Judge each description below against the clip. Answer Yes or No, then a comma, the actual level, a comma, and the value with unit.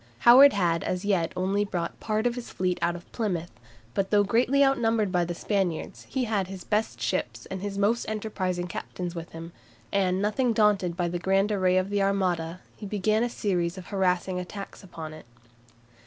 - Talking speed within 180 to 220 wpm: Yes, average, 190 wpm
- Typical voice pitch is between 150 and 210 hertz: Yes, high, 190 Hz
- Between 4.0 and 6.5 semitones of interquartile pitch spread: No, average, 3.0 semitones